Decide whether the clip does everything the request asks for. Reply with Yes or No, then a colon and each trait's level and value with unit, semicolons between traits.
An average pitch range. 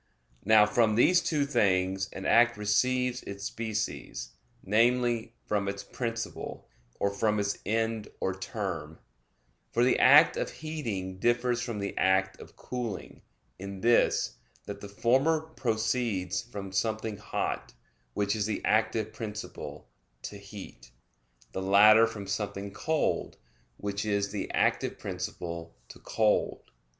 Yes: average, 3.2 semitones